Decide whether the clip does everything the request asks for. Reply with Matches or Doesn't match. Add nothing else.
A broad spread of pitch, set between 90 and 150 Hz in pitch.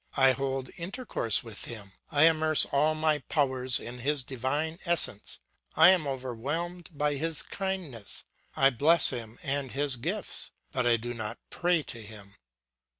Doesn't match